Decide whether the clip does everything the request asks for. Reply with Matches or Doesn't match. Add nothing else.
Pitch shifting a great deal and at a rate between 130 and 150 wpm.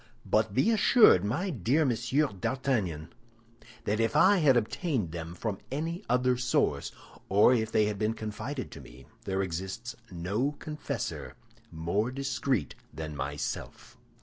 Matches